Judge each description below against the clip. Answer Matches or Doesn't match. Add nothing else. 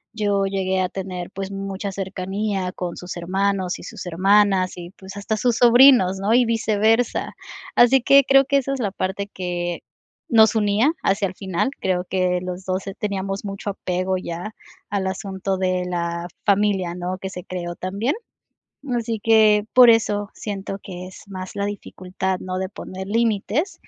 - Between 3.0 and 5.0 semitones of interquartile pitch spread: Doesn't match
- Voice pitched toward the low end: Doesn't match